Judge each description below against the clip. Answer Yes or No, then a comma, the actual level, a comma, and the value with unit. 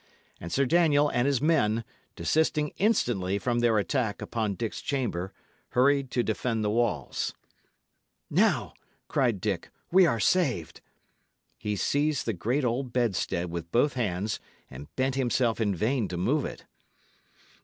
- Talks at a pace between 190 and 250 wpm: No, average, 145 wpm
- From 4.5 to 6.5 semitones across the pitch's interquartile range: Yes, average, 5.2 semitones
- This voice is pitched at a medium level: No, low, 120 Hz